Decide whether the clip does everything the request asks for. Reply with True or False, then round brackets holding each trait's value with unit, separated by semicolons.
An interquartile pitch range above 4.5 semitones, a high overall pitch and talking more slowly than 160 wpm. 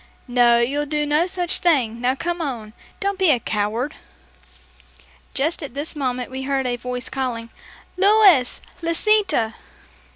True (5.5 semitones; 270 Hz; 140 wpm)